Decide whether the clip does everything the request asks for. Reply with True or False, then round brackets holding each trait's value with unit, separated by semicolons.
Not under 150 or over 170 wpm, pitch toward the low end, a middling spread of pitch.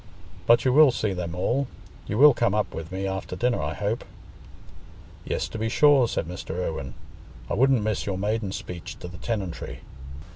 False (180 wpm; 105 Hz; 4.7 semitones)